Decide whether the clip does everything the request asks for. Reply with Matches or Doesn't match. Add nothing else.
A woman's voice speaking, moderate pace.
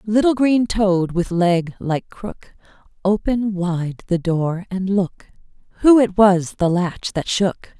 Matches